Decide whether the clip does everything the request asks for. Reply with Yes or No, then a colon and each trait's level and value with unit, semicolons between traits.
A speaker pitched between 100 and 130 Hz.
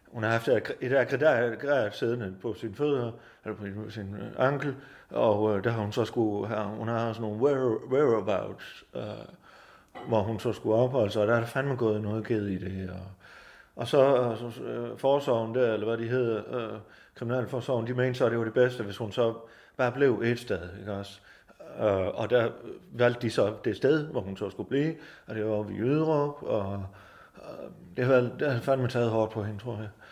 Yes: low, 115 Hz